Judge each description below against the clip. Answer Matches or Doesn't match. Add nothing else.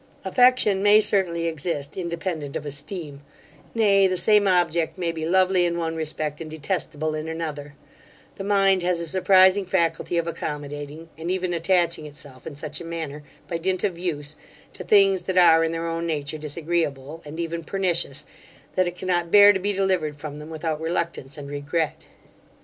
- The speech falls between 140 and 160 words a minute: Doesn't match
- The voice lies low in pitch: Doesn't match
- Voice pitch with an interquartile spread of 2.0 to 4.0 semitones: Matches